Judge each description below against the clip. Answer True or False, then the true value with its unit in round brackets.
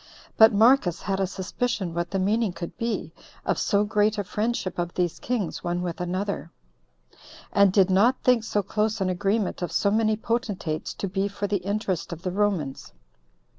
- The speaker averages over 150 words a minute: True (180 wpm)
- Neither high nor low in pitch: False (200 Hz)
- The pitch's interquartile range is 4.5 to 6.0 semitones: False (3.0 semitones)